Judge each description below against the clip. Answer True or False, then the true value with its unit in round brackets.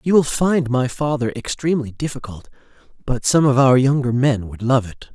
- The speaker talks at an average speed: True (185 wpm)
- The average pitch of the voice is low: True (130 Hz)